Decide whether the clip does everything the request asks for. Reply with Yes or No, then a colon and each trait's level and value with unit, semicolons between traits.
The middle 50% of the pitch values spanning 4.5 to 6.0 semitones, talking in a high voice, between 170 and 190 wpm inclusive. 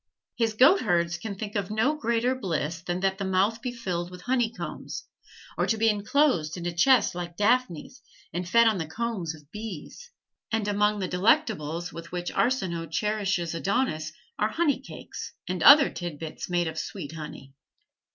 Yes: average, 5.0 semitones; high, 195 Hz; average, 175 wpm